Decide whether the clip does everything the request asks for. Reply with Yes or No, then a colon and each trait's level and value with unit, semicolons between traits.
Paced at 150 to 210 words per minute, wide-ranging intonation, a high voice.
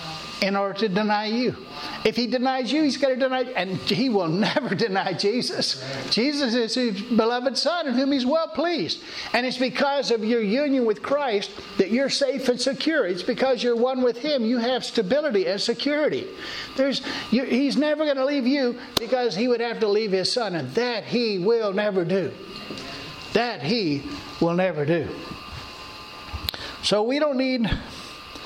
No: average, 180 wpm; average, 4.4 semitones; high, 245 Hz